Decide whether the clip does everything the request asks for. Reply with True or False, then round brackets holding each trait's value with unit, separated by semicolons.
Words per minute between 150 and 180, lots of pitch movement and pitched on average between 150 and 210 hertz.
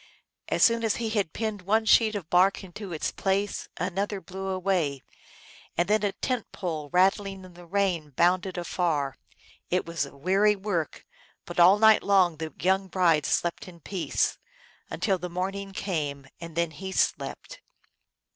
False (165 wpm; 2.8 semitones; 185 Hz)